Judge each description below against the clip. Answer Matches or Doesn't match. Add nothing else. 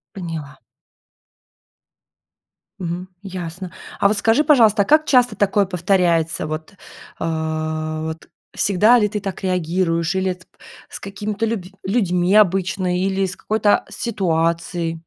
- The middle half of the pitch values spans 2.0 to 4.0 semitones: Matches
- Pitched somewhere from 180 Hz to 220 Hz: Matches